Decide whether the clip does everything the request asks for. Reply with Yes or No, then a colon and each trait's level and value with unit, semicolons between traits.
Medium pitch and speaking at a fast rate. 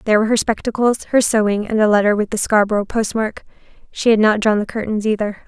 No: high, 215 Hz; fast, 220 wpm